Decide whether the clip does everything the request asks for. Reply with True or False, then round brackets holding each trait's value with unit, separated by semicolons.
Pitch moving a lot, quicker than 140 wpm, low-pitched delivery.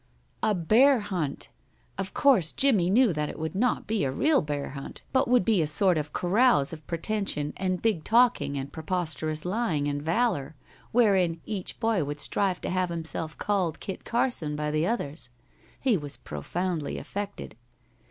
False (6.2 semitones; 170 wpm; 180 Hz)